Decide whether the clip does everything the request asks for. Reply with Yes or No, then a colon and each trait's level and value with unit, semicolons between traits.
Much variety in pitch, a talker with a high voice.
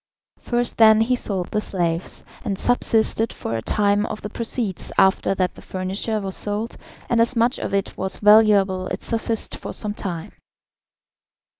No: average, 2.9 semitones; high, 210 Hz